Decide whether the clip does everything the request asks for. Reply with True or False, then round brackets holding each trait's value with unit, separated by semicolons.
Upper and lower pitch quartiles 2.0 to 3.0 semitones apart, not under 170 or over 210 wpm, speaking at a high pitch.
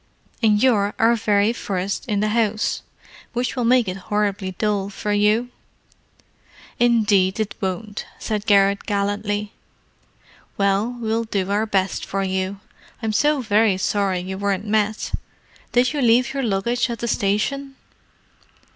False (2.5 semitones; 140 wpm; 210 Hz)